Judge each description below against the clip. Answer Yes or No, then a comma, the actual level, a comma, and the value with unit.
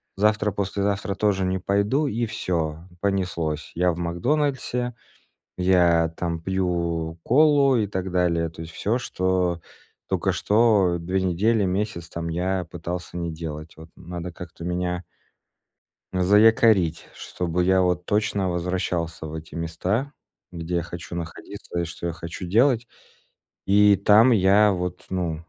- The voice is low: Yes, very low, 90 Hz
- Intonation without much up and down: No, average, 3.2 semitones